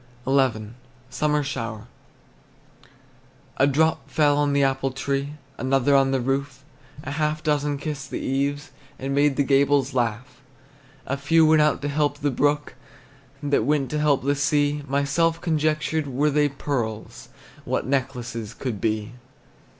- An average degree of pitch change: No, narrow, 1.8 semitones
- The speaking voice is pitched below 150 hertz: Yes, medium, 140 Hz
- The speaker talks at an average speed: Yes, average, 150 wpm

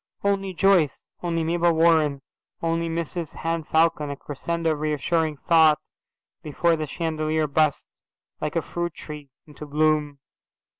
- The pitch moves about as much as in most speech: No, narrow, 1.8 semitones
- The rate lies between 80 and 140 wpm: Yes, slow, 135 wpm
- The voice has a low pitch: No, medium, 160 Hz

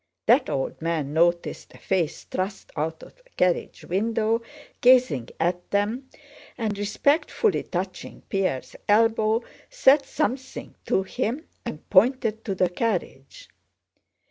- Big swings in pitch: Yes, wide, 5.7 semitones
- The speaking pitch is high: Yes, high, 205 Hz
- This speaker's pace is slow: Yes, slow, 120 wpm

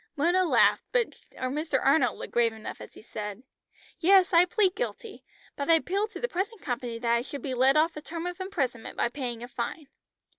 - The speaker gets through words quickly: Yes, fast, 210 wpm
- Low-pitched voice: No, very high, 300 Hz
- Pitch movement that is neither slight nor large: No, wide, 6.9 semitones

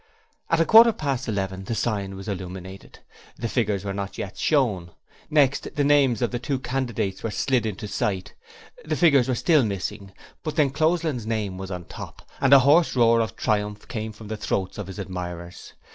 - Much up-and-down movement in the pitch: Yes, wide, 5.7 semitones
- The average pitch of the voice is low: Yes, low, 110 Hz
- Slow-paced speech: No, average, 190 wpm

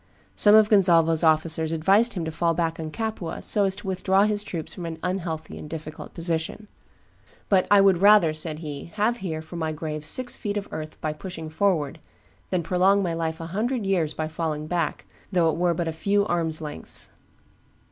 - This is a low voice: No, medium, 170 Hz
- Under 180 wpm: No, average, 200 wpm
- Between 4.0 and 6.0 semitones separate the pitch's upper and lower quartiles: No, average, 3.6 semitones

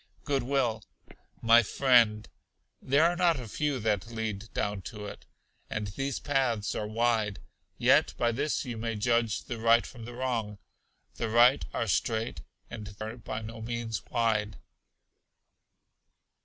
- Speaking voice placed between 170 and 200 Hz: No, low, 115 Hz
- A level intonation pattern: Yes, narrow, 2.3 semitones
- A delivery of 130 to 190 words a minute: Yes, average, 145 wpm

